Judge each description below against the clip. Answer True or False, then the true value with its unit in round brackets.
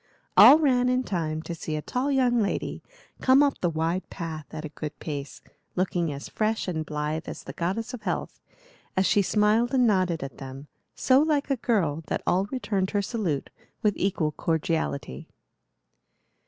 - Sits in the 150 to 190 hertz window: True (185 Hz)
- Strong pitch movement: True (7.3 semitones)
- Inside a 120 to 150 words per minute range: False (175 wpm)